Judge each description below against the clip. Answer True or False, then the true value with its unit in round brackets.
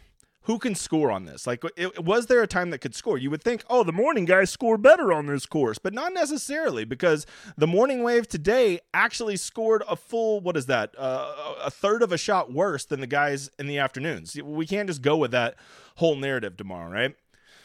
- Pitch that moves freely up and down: True (7.9 semitones)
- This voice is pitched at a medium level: True (180 Hz)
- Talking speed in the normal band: False (220 wpm)